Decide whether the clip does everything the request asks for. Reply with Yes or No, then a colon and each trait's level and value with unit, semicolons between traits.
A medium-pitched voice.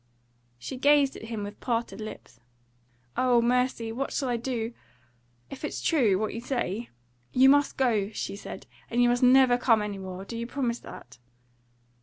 No: high, 240 Hz